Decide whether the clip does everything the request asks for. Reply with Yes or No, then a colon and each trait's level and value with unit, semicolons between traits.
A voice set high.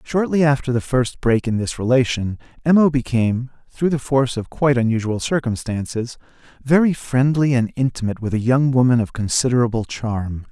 No: low, 125 Hz